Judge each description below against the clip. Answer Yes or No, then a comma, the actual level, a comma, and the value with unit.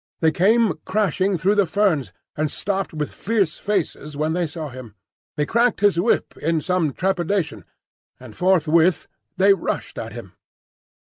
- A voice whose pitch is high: No, medium, 180 Hz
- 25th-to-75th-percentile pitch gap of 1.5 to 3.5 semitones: No, average, 4.3 semitones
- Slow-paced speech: No, average, 150 wpm